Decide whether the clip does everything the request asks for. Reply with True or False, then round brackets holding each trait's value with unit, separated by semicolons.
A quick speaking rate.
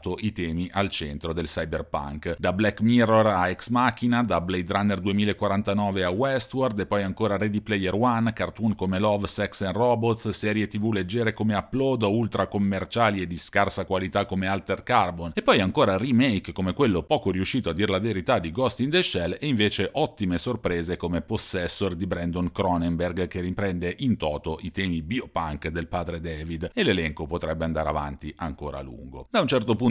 True (185 wpm)